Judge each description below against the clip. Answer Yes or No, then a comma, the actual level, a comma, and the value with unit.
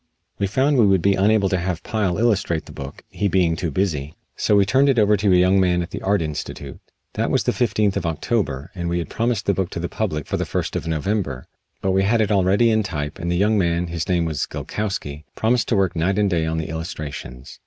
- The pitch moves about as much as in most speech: Yes, average, 4.0 semitones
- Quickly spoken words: Yes, fast, 250 wpm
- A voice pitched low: Yes, very low, 95 Hz